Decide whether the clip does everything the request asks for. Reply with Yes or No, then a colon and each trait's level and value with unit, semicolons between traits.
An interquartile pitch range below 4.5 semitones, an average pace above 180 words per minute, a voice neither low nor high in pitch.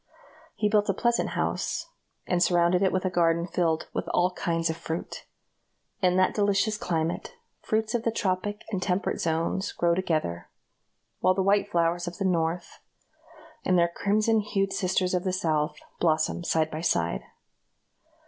No: average, 2.9 semitones; average, 160 wpm; medium, 180 Hz